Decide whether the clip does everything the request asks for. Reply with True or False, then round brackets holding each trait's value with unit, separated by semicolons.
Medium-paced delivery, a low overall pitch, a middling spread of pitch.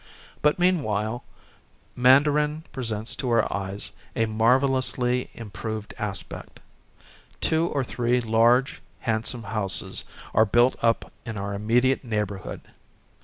False (120 wpm; 115 Hz; 3.1 semitones)